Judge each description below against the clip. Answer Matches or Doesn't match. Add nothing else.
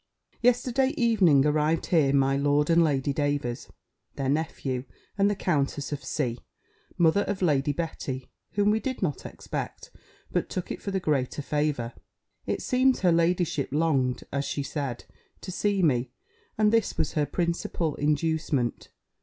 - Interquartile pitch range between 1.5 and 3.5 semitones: Doesn't match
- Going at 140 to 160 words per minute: Matches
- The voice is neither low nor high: Matches